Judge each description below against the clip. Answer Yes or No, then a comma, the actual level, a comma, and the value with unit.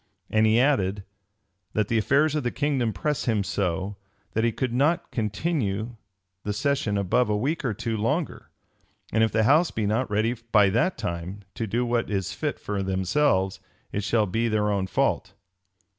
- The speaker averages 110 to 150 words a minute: No, average, 180 wpm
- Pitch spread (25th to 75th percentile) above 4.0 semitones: No, average, 3.7 semitones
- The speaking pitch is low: Yes, low, 110 Hz